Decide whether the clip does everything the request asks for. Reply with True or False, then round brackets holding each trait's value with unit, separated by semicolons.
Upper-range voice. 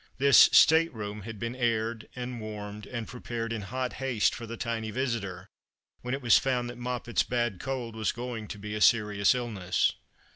False (115 Hz)